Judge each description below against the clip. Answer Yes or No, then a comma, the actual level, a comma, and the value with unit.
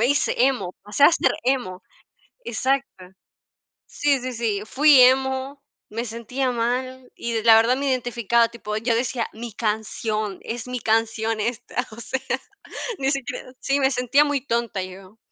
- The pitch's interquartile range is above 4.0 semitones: No, average, 2.9 semitones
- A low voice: No, high, 240 Hz